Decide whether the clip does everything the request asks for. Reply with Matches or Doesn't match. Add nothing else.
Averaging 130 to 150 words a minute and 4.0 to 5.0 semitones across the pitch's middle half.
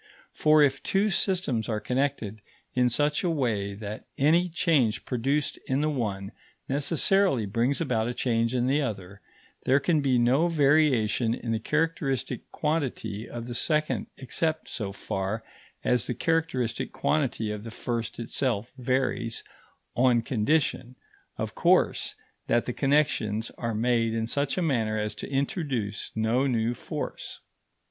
Matches